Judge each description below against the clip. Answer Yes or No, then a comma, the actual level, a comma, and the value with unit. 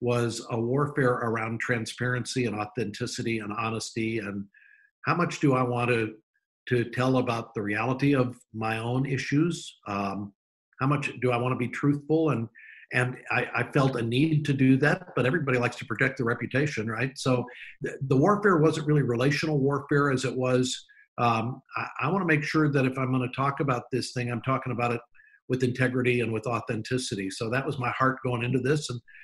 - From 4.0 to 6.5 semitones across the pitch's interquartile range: No, average, 3.1 semitones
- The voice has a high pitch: No, low, 125 Hz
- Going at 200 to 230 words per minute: Yes, fast, 205 wpm